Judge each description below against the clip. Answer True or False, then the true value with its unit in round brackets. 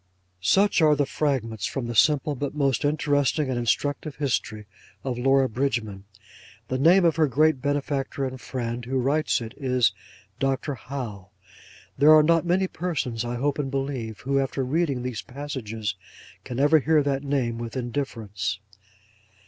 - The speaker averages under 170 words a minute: True (160 wpm)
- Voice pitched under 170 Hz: True (135 Hz)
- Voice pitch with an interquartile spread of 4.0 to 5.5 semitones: False (3.3 semitones)